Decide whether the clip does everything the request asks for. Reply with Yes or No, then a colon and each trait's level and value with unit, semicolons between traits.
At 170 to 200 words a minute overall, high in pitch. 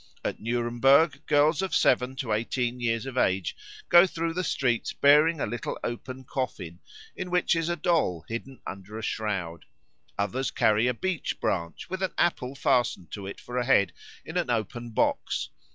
No: average, 175 wpm; low, 125 Hz